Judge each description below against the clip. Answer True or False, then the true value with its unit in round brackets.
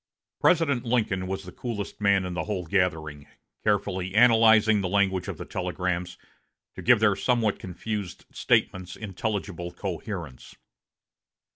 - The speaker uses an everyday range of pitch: True (3.2 semitones)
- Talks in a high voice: False (100 Hz)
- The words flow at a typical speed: False (130 wpm)